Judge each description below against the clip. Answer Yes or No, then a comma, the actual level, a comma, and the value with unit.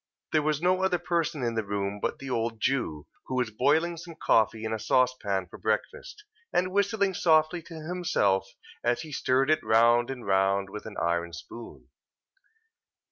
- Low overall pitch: Yes, low, 125 Hz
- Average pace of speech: Yes, average, 175 wpm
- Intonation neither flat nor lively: No, wide, 7.6 semitones